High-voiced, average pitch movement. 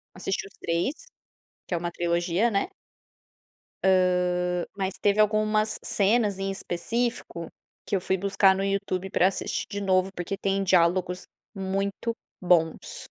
No: high, 195 Hz; narrow, 2.0 semitones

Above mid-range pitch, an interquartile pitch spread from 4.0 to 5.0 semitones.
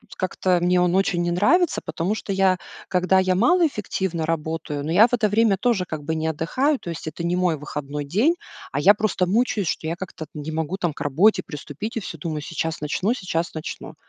No: medium, 180 Hz; average, 4.3 semitones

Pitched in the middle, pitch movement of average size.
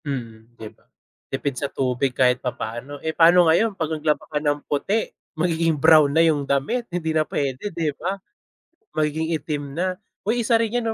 Yes: medium, 155 Hz; average, 3.6 semitones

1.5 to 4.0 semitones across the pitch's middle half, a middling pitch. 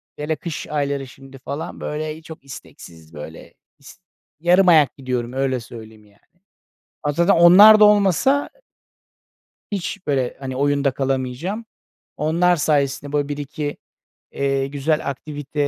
Yes: average, 3.5 semitones; medium, 145 Hz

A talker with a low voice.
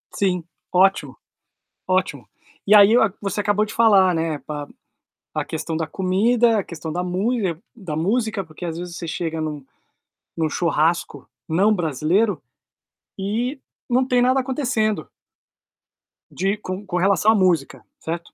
No: medium, 185 Hz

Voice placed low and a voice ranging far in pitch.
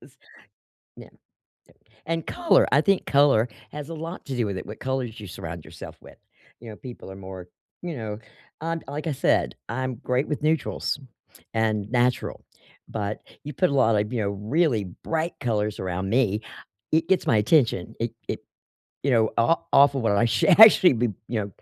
Yes: low, 120 Hz; wide, 5.9 semitones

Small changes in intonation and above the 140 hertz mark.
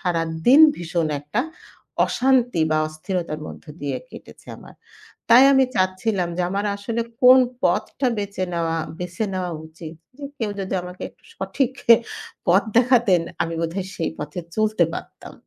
No: average, 5.3 semitones; medium, 185 Hz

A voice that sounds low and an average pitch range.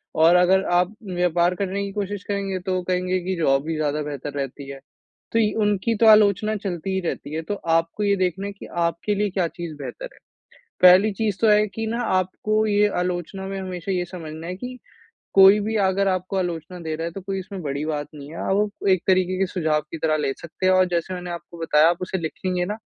No: medium, 185 Hz; average, 3.0 semitones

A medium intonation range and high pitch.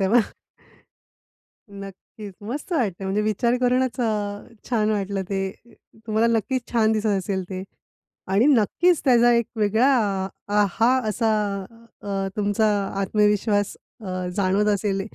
Yes: average, 3.1 semitones; high, 210 Hz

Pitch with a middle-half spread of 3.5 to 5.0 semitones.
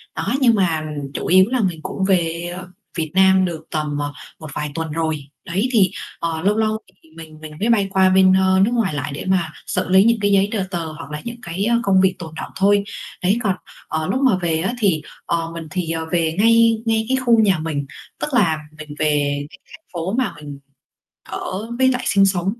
Yes: average, 4.2 semitones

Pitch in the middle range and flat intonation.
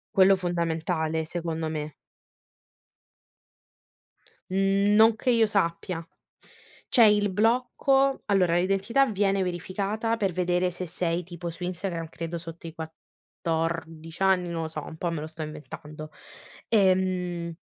No: medium, 180 Hz; average, 3.1 semitones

